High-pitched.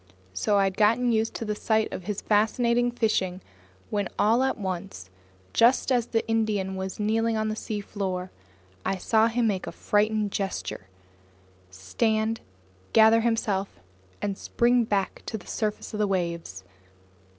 Yes: high, 210 Hz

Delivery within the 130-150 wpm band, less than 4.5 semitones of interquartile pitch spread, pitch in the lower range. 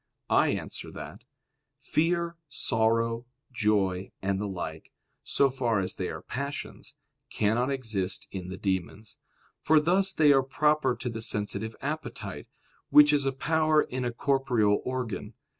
No: average, 140 wpm; wide, 5.5 semitones; low, 120 Hz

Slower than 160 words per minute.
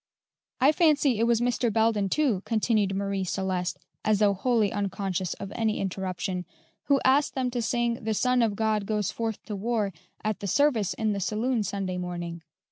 No: average, 180 wpm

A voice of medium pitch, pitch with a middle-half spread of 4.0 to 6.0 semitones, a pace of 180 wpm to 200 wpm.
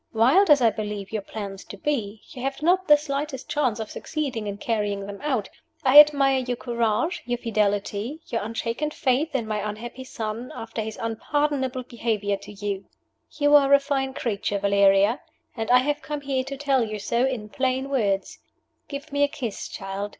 No: high, 240 Hz; average, 4.9 semitones; average, 185 wpm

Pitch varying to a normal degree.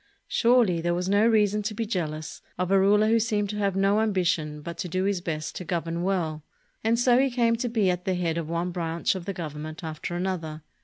Yes: average, 3.9 semitones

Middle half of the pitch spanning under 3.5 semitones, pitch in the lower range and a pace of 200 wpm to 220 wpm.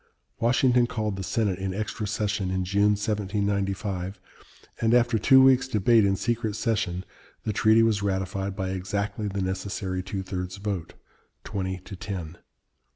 No: narrow, 2.5 semitones; low, 100 Hz; average, 150 wpm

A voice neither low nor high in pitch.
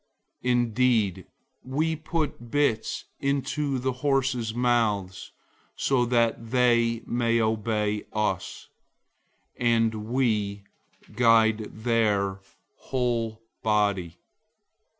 No: low, 115 Hz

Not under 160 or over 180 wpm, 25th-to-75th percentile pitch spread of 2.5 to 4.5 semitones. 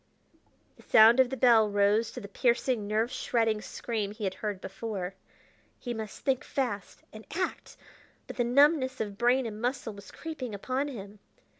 Yes: average, 170 wpm; average, 3.5 semitones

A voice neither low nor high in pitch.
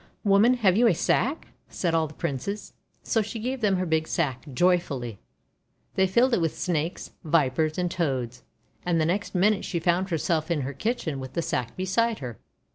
Yes: medium, 170 Hz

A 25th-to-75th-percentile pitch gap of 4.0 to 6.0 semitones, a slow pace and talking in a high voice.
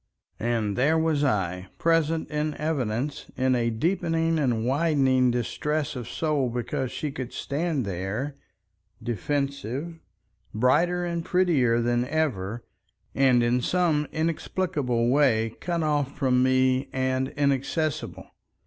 No: average, 4.4 semitones; slow, 120 wpm; low, 135 Hz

